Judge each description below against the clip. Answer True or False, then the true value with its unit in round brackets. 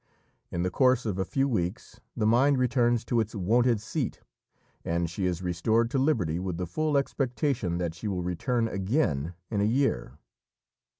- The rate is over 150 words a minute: True (175 wpm)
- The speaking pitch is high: False (110 Hz)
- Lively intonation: True (6.1 semitones)